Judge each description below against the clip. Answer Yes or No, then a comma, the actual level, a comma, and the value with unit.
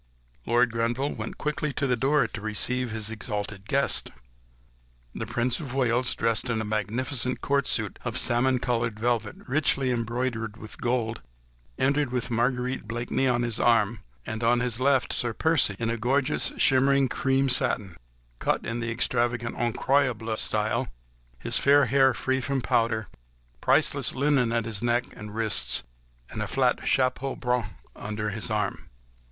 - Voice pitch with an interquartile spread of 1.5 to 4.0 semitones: Yes, narrow, 2.6 semitones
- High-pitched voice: No, low, 120 Hz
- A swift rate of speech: No, average, 155 wpm